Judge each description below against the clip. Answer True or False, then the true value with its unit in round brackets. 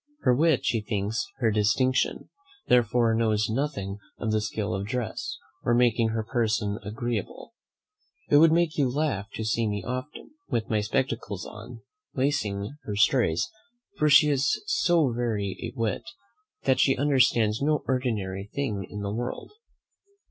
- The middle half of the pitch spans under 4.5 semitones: True (4.0 semitones)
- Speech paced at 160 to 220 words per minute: False (150 wpm)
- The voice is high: False (115 Hz)